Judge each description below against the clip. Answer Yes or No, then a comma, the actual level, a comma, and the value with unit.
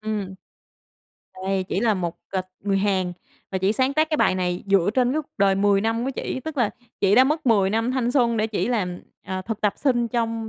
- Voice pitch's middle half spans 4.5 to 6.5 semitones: No, average, 4.0 semitones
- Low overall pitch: No, high, 215 Hz